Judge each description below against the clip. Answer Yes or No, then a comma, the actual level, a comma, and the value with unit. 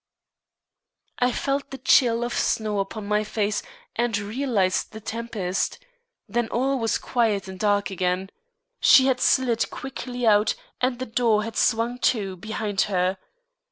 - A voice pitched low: No, high, 220 Hz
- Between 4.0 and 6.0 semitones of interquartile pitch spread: No, average, 3.3 semitones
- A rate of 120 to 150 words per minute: Yes, average, 145 wpm